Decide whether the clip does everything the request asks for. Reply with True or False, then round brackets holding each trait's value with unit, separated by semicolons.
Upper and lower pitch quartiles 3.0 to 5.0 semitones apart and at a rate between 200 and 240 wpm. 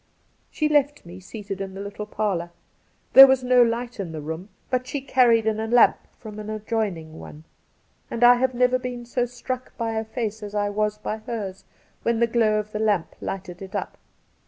True (3.3 semitones; 205 wpm)